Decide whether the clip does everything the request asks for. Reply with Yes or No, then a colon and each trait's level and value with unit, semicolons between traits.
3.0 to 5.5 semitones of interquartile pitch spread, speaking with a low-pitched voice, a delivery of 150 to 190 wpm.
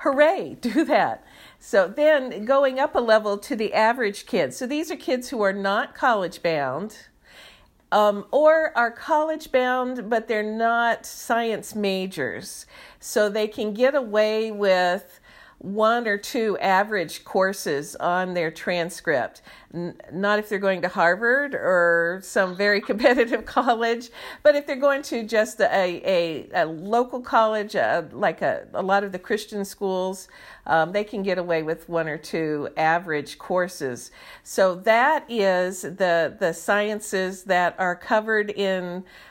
No: average, 4.6 semitones; high, 210 Hz; average, 155 wpm